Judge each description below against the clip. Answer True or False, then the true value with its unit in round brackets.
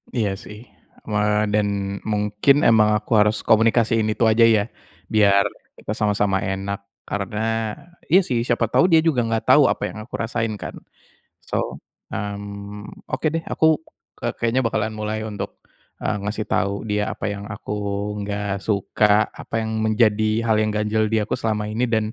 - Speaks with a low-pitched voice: True (105 Hz)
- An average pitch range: False (1.5 semitones)